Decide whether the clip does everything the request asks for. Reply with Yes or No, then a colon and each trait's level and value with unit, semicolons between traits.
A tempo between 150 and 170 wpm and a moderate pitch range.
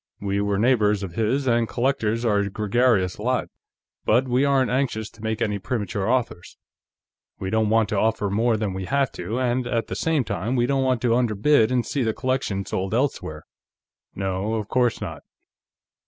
No: average, 185 wpm; average, 3.7 semitones